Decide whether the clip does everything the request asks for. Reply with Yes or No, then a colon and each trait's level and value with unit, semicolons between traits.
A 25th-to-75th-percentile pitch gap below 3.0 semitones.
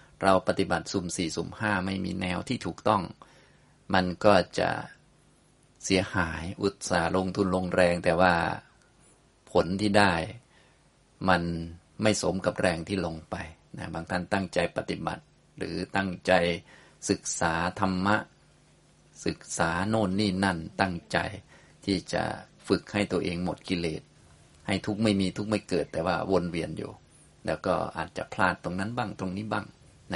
Yes: narrow, 2.6 semitones